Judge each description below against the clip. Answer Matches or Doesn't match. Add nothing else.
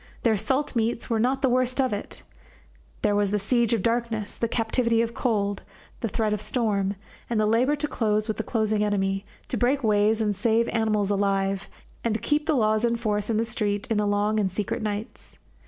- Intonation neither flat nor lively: Doesn't match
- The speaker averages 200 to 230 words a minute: Matches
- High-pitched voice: Matches